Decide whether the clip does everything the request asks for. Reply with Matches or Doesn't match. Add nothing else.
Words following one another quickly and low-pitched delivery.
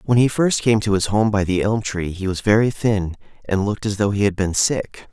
Matches